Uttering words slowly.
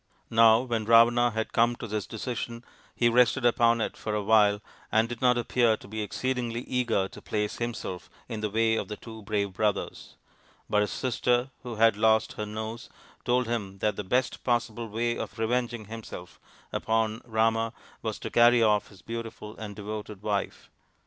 No: average, 180 wpm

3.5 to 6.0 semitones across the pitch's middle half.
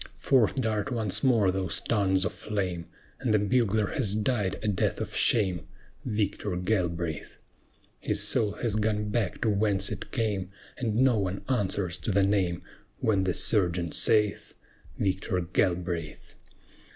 No: average, 2.9 semitones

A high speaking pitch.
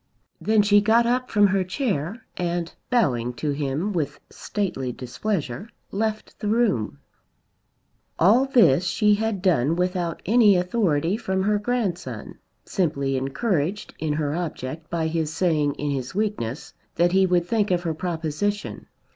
No: medium, 180 Hz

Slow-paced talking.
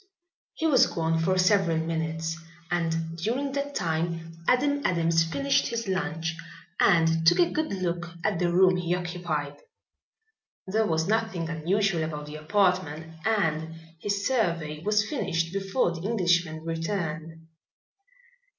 Yes: slow, 130 wpm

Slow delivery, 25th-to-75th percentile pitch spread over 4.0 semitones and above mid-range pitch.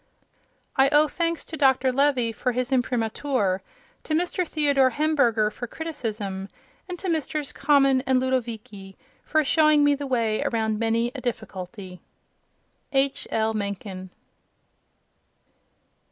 Yes: slow, 125 wpm; average, 4.9 semitones; very high, 255 Hz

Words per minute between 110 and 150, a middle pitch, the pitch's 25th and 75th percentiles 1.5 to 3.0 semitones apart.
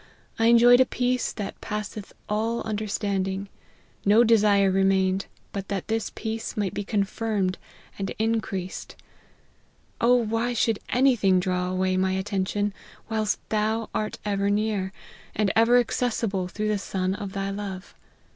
No: average, 140 wpm; high, 205 Hz; narrow, 2.6 semitones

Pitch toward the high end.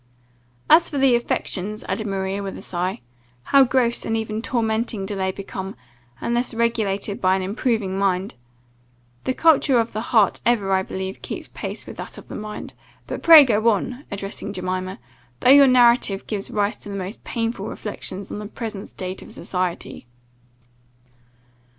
Yes: high, 210 Hz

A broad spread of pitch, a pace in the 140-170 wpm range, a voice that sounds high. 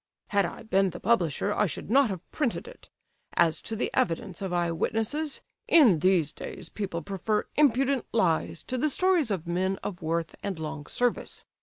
No: wide, 6.2 semitones; average, 180 wpm; high, 200 Hz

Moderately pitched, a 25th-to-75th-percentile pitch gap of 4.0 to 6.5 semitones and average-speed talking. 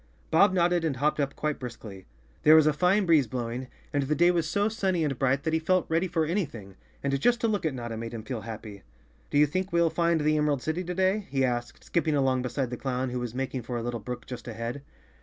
No: medium, 145 Hz; wide, 5.5 semitones; fast, 250 wpm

